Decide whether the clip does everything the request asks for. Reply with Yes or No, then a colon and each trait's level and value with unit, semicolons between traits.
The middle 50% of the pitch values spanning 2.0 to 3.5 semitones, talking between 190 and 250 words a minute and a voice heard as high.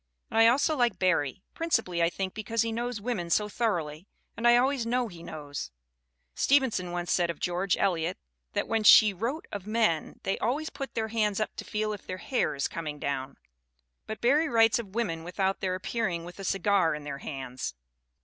No: average, 5.2 semitones; average, 195 wpm; high, 200 Hz